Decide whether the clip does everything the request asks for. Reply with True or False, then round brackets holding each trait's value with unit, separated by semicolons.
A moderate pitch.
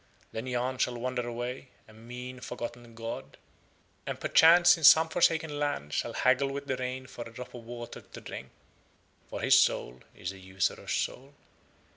False (125 Hz)